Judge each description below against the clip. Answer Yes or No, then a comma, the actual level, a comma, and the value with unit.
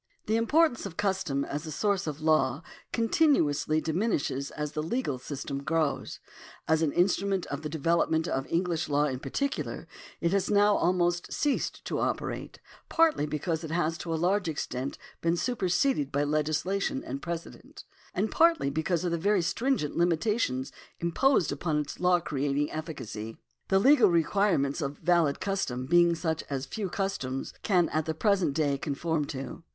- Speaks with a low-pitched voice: No, medium, 165 Hz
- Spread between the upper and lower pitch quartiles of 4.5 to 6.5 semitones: Yes, average, 4.9 semitones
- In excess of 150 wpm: Yes, average, 165 wpm